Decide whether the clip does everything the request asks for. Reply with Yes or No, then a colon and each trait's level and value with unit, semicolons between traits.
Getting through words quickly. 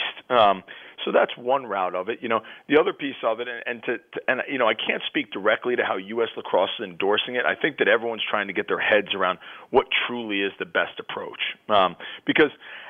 Yes: fast, 250 wpm